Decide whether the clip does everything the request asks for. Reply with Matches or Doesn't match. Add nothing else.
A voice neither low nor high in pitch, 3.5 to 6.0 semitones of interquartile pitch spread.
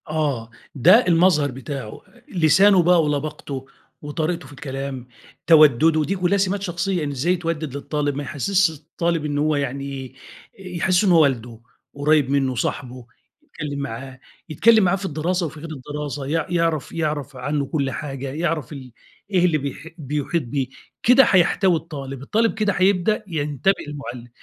Matches